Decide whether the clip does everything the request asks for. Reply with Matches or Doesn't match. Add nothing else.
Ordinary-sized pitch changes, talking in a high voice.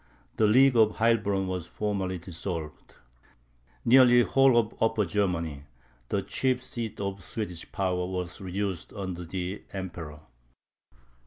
Doesn't match